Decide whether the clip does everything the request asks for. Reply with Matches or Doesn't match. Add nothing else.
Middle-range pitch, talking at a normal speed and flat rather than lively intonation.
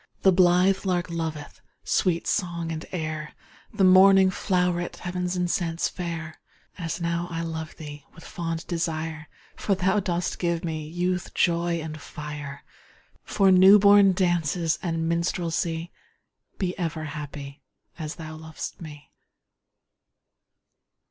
Doesn't match